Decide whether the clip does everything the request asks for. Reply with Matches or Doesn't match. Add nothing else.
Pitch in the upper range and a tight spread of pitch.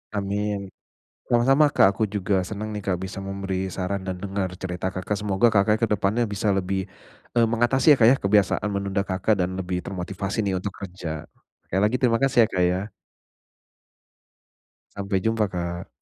Doesn't match